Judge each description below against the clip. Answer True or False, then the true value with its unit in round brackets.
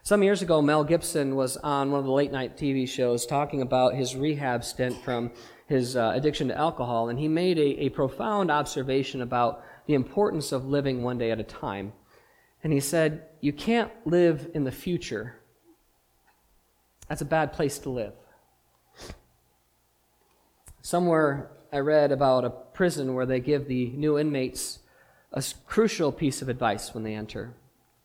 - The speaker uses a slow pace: False (165 wpm)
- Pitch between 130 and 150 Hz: True (140 Hz)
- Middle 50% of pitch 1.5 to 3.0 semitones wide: False (3.7 semitones)